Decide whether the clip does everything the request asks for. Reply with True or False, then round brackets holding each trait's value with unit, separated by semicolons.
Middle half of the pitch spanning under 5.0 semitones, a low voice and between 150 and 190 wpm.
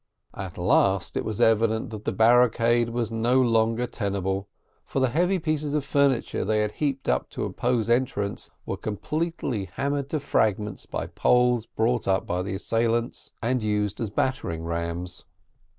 True (3.9 semitones; 115 Hz; 160 wpm)